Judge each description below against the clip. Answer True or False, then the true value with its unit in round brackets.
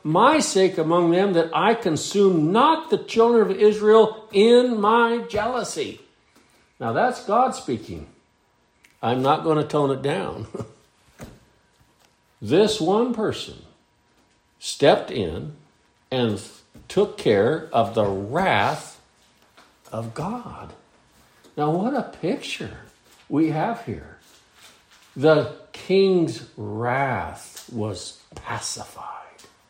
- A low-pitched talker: False (170 Hz)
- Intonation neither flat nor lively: False (7.9 semitones)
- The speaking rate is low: True (105 wpm)